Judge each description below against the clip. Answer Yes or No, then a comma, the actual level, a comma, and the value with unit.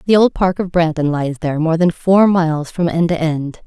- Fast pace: Yes, fast, 245 wpm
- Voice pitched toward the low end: No, medium, 165 Hz